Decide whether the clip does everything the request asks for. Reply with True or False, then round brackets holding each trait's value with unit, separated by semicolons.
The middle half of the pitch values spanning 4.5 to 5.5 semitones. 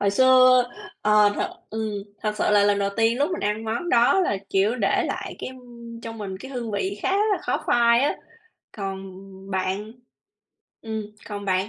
False (3.1 semitones)